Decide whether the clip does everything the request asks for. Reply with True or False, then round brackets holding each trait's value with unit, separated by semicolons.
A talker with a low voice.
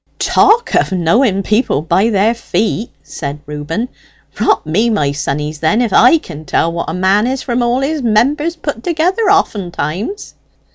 False (215 Hz)